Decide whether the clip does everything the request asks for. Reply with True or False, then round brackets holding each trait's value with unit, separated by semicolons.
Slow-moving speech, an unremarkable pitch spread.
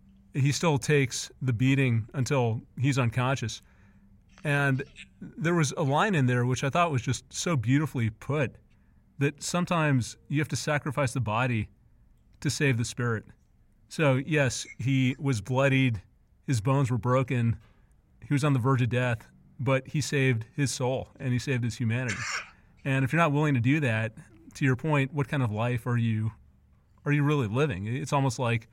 False (180 wpm; 3.6 semitones)